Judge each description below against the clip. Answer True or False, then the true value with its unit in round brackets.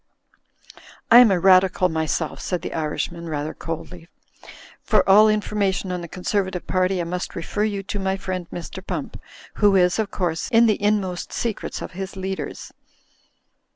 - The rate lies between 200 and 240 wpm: False (160 wpm)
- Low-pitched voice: False (185 Hz)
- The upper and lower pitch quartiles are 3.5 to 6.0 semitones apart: False (2.6 semitones)